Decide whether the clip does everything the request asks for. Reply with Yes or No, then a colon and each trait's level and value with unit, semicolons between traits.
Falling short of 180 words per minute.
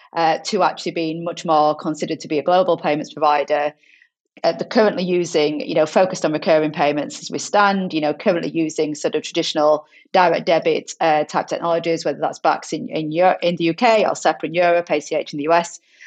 No: fast, 205 wpm